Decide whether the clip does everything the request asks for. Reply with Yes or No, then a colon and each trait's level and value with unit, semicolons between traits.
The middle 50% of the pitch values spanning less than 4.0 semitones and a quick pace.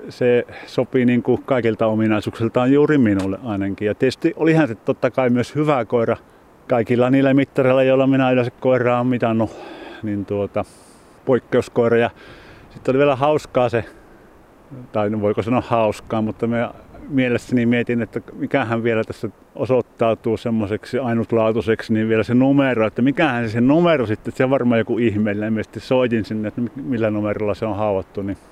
Yes: average, 2.8 semitones; fast, 160 wpm